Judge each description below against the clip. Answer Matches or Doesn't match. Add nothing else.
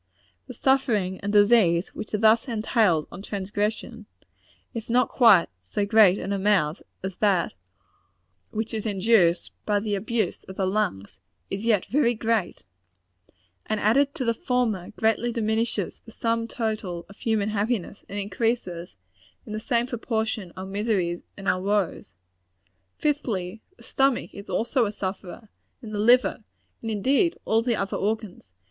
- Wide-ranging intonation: Doesn't match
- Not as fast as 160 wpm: Matches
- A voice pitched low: Doesn't match